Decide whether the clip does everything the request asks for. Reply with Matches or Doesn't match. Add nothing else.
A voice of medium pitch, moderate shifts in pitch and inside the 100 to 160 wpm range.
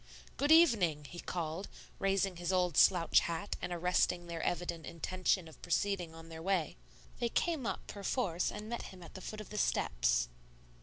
Doesn't match